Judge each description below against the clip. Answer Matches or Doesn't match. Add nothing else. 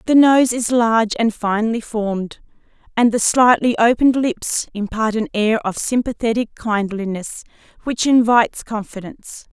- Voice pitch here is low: Doesn't match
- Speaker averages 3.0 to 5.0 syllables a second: Matches